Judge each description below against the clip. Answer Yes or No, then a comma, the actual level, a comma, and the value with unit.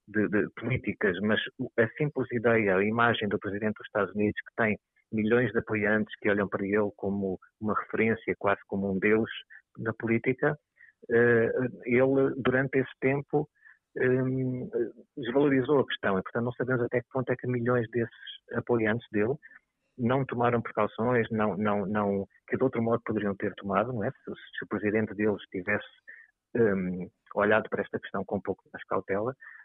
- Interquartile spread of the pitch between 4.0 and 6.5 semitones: No, average, 3.3 semitones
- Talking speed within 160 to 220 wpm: Yes, average, 170 wpm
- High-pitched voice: No, low, 115 Hz